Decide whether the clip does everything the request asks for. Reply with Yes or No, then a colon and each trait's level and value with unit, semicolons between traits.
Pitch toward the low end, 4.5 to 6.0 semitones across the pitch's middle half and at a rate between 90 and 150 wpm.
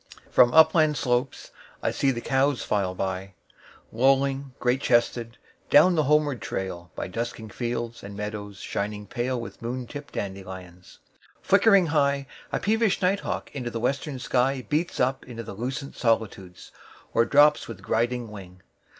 Yes: low, 120 Hz; average, 5.0 semitones; slow, 135 wpm